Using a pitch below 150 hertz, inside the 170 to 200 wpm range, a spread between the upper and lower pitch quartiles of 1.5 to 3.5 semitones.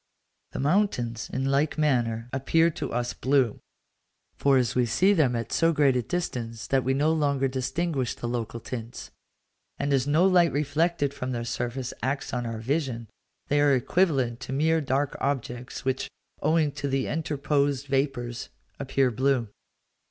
No: low, 135 Hz; average, 160 wpm; average, 3.2 semitones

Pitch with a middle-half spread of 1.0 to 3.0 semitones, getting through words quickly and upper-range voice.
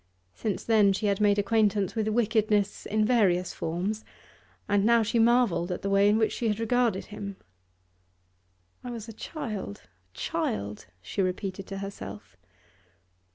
No: narrow, 2.5 semitones; average, 155 wpm; high, 205 Hz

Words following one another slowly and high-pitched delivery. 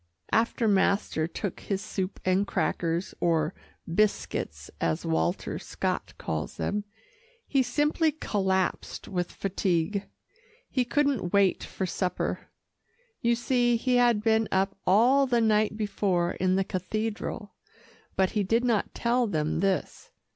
Yes: slow, 130 wpm; high, 205 Hz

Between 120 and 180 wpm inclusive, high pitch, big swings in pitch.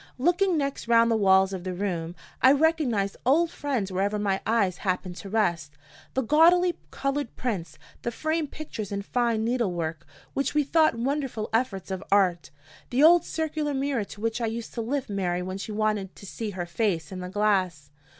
No: average, 190 wpm; high, 220 Hz; wide, 6.4 semitones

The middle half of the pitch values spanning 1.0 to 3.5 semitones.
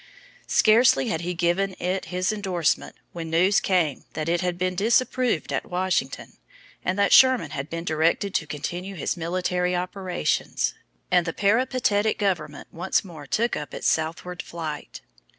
Yes: average, 3.0 semitones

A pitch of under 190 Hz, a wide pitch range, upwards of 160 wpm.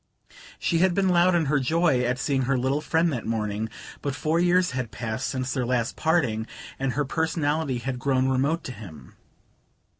No: low, 135 Hz; average, 4.6 semitones; average, 185 wpm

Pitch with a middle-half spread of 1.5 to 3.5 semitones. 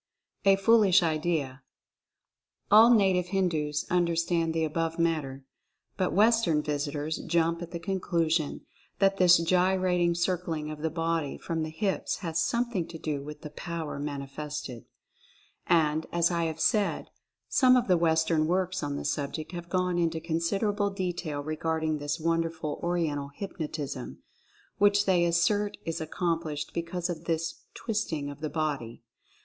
Yes: average, 2.9 semitones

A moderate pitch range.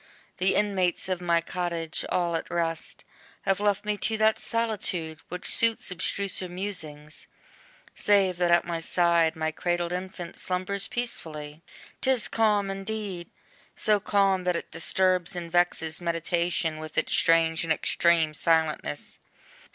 Yes: average, 3.0 semitones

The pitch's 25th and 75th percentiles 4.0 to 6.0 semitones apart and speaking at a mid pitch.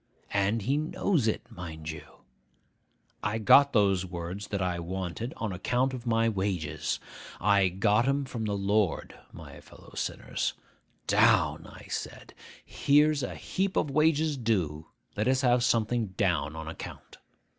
No: wide, 5.6 semitones; low, 105 Hz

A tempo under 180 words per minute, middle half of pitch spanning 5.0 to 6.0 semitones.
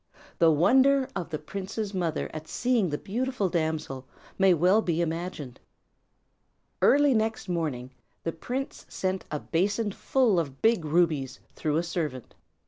Yes: average, 140 wpm; wide, 5.6 semitones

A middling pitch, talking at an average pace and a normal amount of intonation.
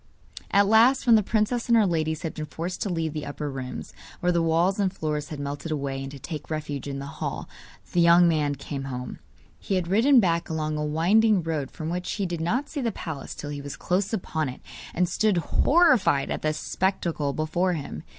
No: medium, 165 Hz; fast, 220 wpm; average, 4.5 semitones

